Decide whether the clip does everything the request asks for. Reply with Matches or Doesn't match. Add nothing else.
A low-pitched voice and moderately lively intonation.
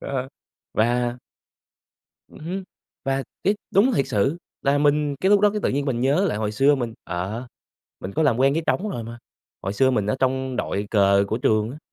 Matches